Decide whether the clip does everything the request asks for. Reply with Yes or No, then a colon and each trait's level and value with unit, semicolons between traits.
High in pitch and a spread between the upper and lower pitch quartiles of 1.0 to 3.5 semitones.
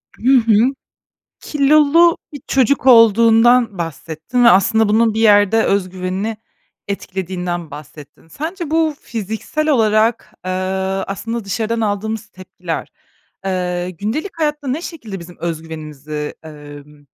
No: high, 215 Hz; wide, 5.4 semitones